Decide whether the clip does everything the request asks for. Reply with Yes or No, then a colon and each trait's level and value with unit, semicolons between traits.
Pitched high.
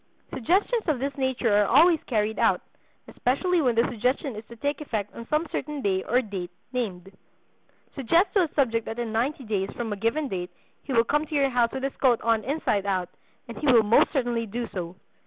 Yes: high, 240 Hz